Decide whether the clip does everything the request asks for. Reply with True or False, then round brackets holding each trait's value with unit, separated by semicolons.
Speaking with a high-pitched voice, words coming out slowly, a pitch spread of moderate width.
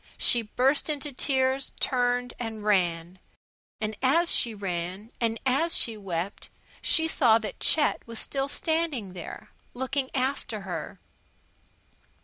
True (245 Hz; 125 wpm; 4.7 semitones)